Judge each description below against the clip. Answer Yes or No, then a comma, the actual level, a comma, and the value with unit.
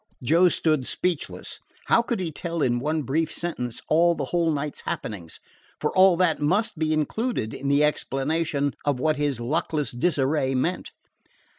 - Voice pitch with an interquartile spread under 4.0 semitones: Yes, average, 3.6 semitones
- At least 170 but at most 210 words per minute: No, average, 160 wpm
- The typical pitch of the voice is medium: Yes, medium, 155 Hz